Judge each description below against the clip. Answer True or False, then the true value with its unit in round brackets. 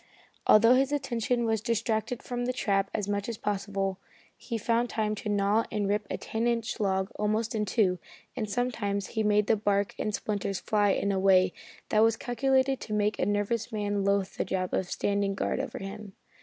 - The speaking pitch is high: True (210 Hz)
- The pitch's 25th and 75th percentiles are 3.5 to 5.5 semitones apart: False (2.4 semitones)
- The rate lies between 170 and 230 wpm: True (195 wpm)